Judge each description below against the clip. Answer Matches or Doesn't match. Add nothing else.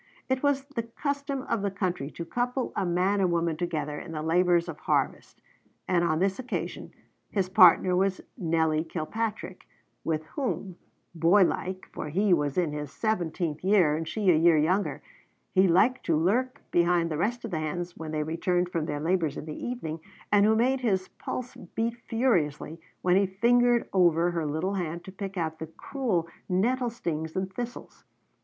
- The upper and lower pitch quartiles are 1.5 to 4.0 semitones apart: Doesn't match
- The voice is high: Doesn't match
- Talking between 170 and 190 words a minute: Matches